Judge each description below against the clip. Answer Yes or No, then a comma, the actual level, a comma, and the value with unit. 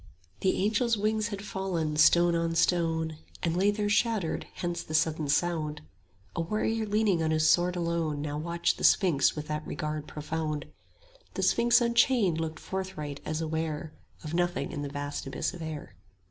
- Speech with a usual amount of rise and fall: Yes, average, 3.8 semitones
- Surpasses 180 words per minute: No, average, 175 wpm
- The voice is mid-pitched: Yes, medium, 165 Hz